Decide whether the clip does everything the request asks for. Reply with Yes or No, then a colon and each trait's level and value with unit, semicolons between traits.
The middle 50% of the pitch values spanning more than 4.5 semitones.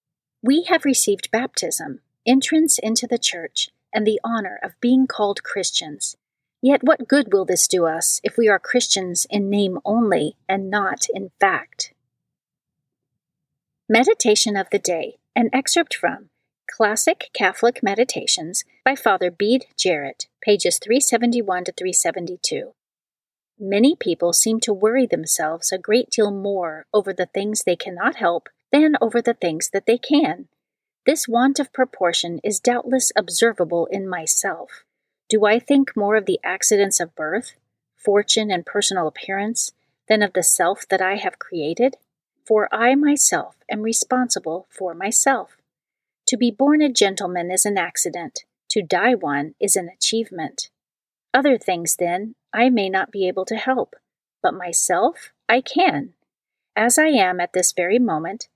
Yes: average, 4.9 semitones